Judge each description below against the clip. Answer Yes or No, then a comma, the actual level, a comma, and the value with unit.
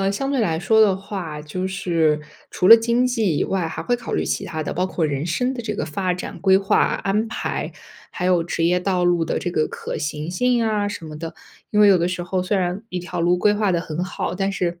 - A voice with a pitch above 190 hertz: No, medium, 185 Hz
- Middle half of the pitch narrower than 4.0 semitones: Yes, average, 3.4 semitones